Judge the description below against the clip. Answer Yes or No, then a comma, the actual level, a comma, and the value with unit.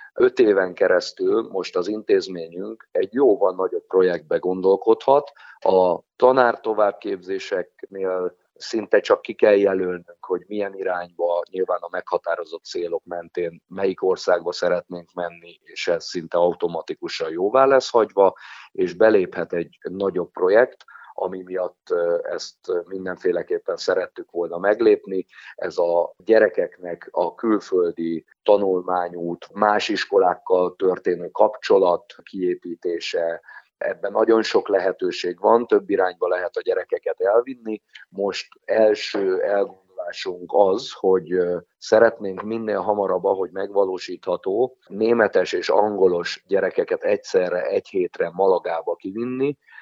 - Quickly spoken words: No, average, 110 wpm